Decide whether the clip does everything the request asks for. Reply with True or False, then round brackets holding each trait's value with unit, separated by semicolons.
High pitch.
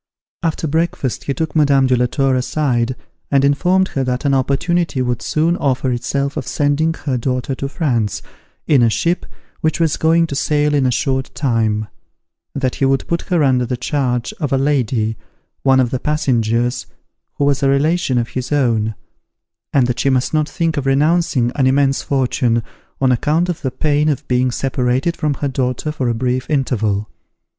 False (135 Hz)